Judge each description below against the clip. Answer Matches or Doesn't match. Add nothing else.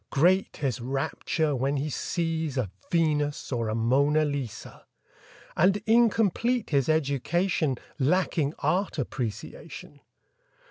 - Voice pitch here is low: Doesn't match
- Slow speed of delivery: Matches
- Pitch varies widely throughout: Doesn't match